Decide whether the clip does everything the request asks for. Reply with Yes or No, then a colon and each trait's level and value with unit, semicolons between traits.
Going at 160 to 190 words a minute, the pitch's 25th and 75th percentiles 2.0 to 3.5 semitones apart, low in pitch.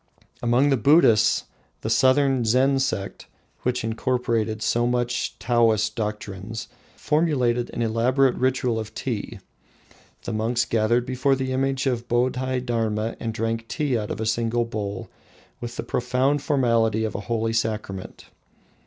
No: average, 145 wpm; narrow, 2.6 semitones; low, 120 Hz